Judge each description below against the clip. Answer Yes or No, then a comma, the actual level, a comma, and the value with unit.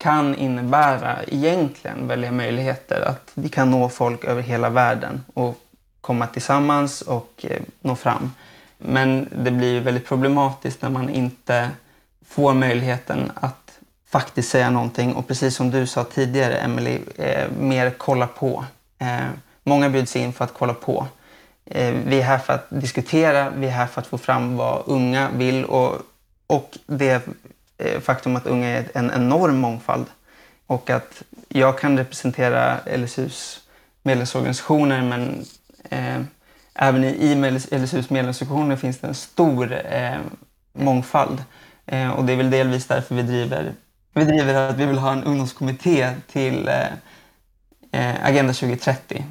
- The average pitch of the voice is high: No, low, 130 Hz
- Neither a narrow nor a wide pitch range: No, narrow, 1.6 semitones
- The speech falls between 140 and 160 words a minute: Yes, average, 145 wpm